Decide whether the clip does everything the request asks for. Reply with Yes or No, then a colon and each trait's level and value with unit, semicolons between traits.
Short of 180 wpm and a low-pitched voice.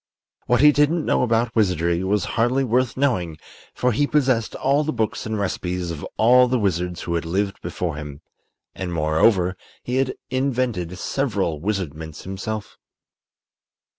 Yes: average, 150 wpm; low, 105 Hz